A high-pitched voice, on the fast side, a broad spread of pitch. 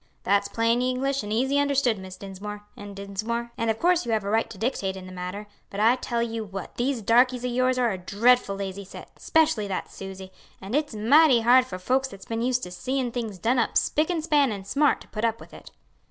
No: high, 230 Hz; fast, 235 wpm; average, 4.2 semitones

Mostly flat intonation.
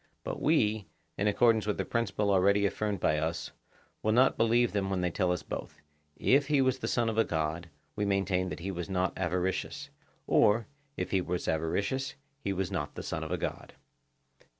No: average, 3.8 semitones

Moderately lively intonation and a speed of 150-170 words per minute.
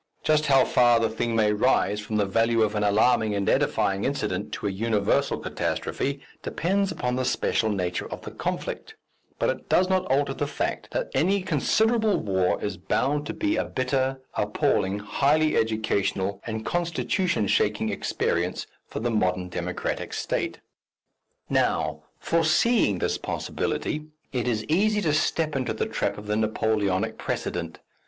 No: wide, 6.7 semitones; average, 155 wpm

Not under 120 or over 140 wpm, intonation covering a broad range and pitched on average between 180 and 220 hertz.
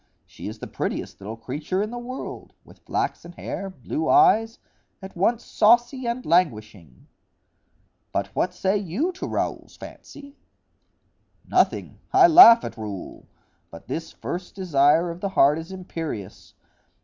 Yes: slow, 135 wpm; wide, 8.1 semitones; high, 190 Hz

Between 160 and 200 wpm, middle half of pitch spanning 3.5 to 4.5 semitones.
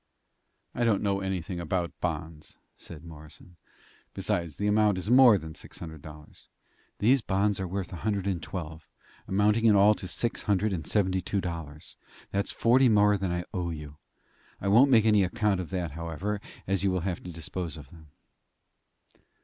Yes: average, 180 wpm; average, 3.8 semitones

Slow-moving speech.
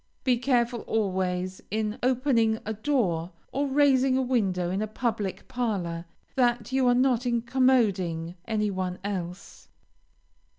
Yes: slow, 130 wpm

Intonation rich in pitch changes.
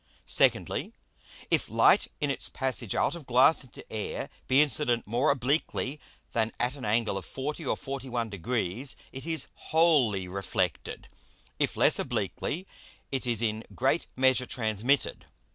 No: average, 3.8 semitones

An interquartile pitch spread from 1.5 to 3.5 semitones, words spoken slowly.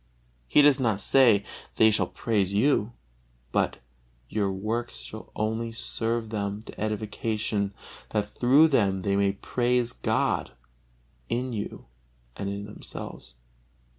Yes: average, 2.8 semitones; slow, 125 wpm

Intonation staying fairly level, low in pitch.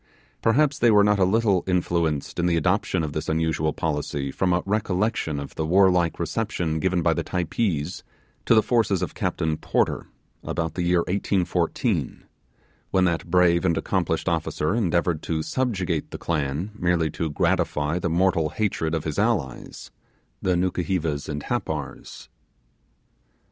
No: average, 3.1 semitones; very low, 85 Hz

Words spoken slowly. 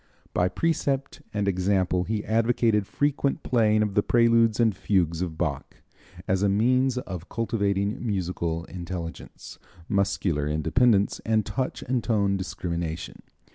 Yes: slow, 130 wpm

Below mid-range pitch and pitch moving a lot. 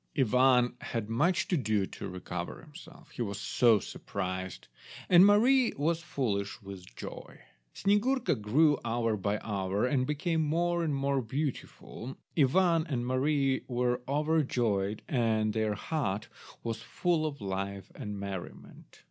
Yes: low, 125 Hz; wide, 6.8 semitones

